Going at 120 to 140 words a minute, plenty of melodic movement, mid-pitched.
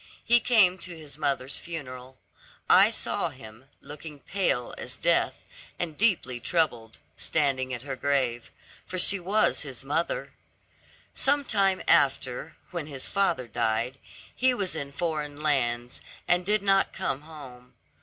Yes: slow, 135 wpm; wide, 6.3 semitones; medium, 150 Hz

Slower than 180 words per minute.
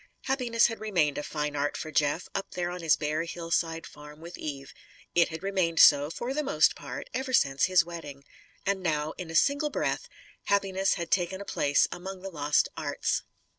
No: average, 195 wpm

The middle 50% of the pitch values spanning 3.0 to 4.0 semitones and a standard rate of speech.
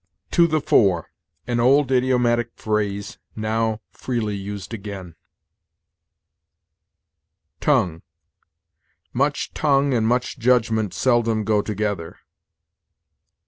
No: average, 3.5 semitones; slow, 90 wpm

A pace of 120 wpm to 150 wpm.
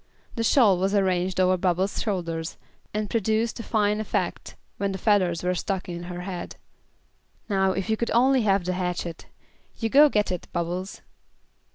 No: average, 170 wpm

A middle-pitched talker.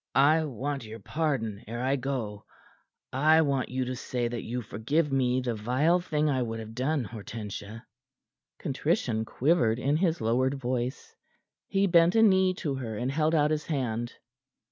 No: low, 130 Hz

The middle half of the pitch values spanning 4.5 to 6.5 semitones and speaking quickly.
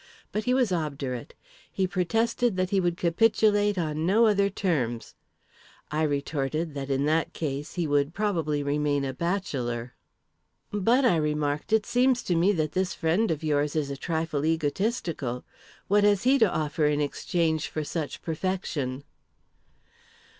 No: wide, 5.4 semitones; average, 155 wpm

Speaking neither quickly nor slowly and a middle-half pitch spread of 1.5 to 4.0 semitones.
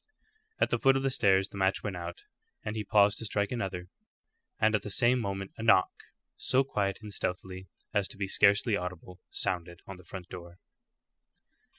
Yes: average, 190 wpm; narrow, 2.5 semitones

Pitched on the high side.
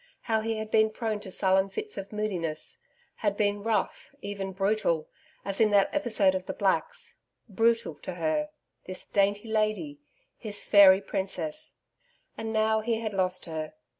Yes: high, 205 Hz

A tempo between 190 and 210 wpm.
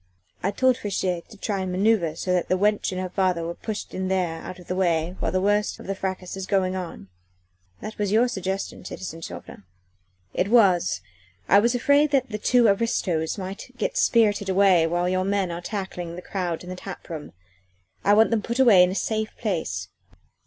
Yes: average, 200 wpm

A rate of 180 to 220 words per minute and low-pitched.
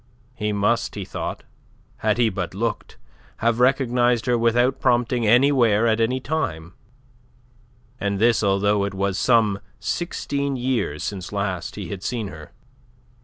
No: average, 140 wpm; low, 115 Hz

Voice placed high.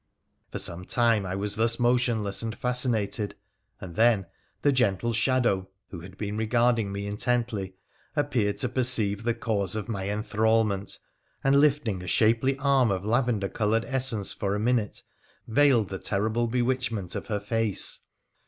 No: low, 110 Hz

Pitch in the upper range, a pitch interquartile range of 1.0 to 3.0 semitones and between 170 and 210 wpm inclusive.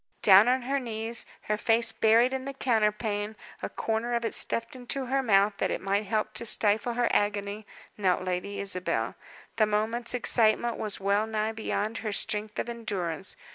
Yes: high, 220 Hz; narrow, 2.4 semitones; average, 175 wpm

